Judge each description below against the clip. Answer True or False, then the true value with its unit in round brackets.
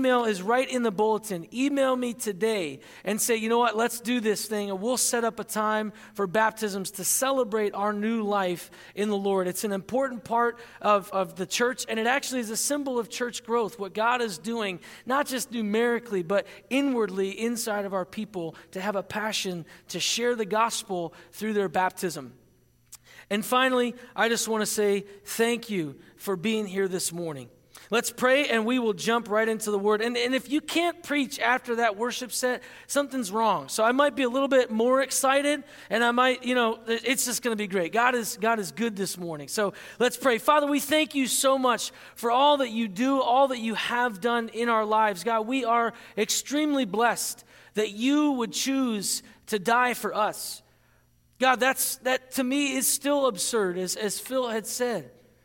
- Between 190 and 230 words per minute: True (200 wpm)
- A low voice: False (230 Hz)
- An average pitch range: True (3.5 semitones)